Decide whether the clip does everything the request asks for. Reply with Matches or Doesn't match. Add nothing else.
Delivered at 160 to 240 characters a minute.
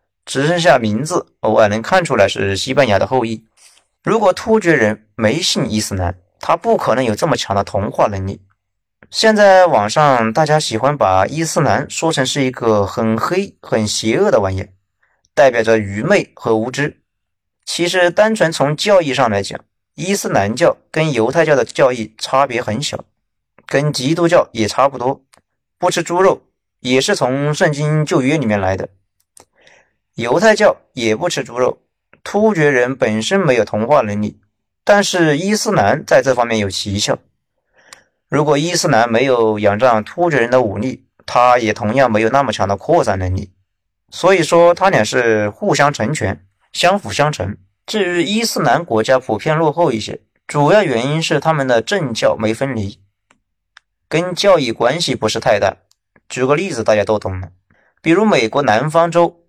Doesn't match